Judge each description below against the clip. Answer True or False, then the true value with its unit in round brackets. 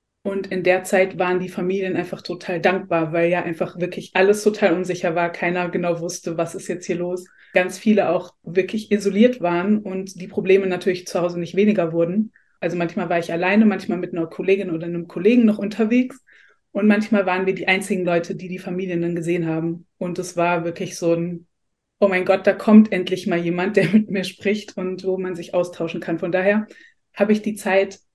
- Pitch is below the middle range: False (185 Hz)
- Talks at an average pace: False (210 wpm)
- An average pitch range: False (2.2 semitones)